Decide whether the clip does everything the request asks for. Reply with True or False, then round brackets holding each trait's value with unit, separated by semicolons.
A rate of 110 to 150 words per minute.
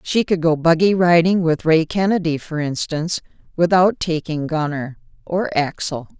True (145 wpm)